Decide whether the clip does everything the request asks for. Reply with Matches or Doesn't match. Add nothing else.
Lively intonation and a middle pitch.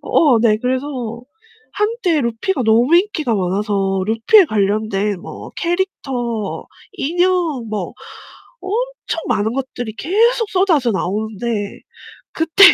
Doesn't match